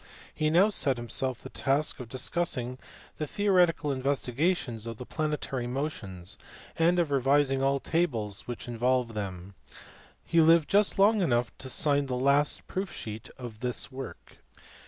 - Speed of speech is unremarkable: Yes, average, 150 wpm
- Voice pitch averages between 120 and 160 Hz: Yes, low, 135 Hz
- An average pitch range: Yes, average, 4.6 semitones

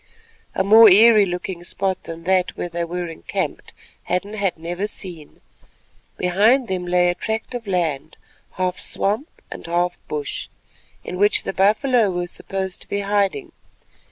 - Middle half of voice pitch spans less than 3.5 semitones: Yes, average, 2.8 semitones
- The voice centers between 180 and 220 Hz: Yes, medium, 185 Hz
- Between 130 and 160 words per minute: Yes, average, 145 wpm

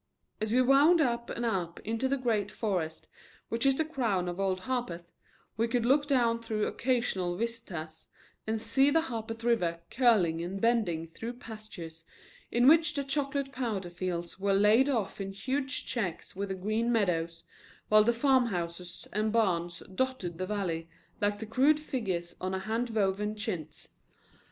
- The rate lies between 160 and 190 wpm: Yes, average, 165 wpm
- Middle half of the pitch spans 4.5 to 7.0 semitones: Yes, average, 5.1 semitones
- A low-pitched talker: No, high, 215 Hz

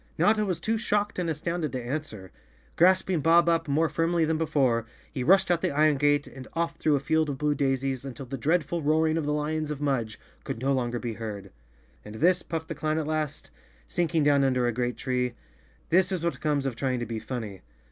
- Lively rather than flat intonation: No, average, 4.3 semitones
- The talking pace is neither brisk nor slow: No, fast, 220 wpm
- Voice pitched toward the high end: No, medium, 150 Hz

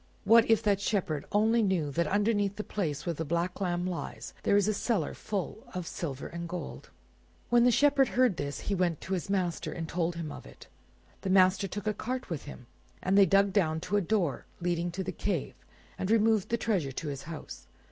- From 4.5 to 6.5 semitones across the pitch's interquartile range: No, average, 3.7 semitones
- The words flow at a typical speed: No, fast, 215 wpm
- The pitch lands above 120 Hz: Yes, medium, 185 Hz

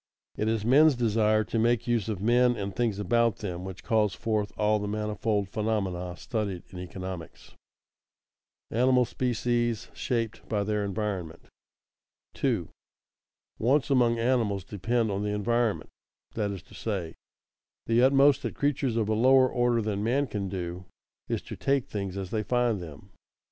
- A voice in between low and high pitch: No, low, 110 Hz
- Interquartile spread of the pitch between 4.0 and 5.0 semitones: No, average, 3.2 semitones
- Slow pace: No, average, 160 wpm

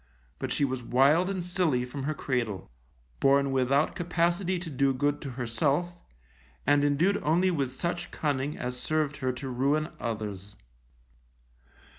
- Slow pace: No, average, 145 wpm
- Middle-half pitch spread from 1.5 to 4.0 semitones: No, average, 4.5 semitones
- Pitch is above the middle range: No, medium, 140 Hz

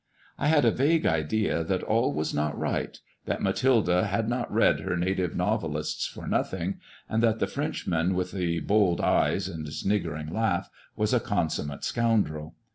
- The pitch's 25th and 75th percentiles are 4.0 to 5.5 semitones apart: Yes, average, 5.2 semitones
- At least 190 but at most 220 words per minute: No, average, 170 wpm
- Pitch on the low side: Yes, very low, 95 Hz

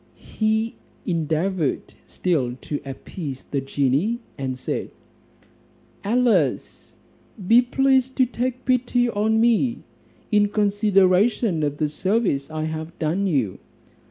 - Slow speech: Yes, slow, 110 wpm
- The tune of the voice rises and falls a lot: Yes, wide, 7.3 semitones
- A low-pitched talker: No, high, 195 Hz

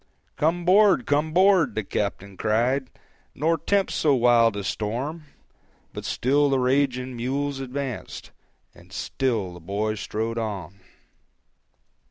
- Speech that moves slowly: Yes, slow, 125 wpm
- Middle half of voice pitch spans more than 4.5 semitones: Yes, average, 4.9 semitones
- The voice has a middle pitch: No, low, 125 Hz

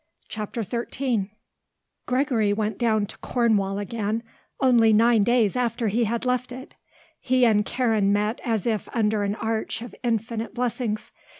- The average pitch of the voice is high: Yes, high, 225 Hz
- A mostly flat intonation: Yes, narrow, 2.3 semitones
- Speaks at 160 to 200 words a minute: No, average, 145 wpm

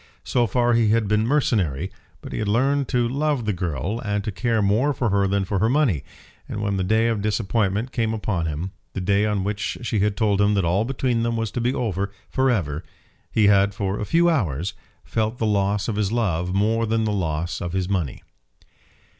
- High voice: No, low, 105 Hz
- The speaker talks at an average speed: No, fast, 220 wpm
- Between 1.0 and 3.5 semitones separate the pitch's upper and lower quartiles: Yes, average, 3.1 semitones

